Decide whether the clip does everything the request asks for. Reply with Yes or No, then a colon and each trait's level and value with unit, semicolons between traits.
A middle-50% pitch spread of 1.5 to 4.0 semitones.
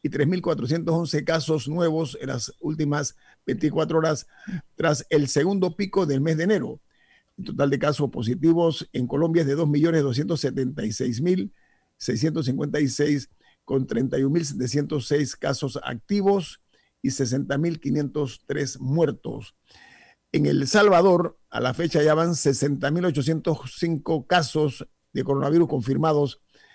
Yes: average, 3.0 semitones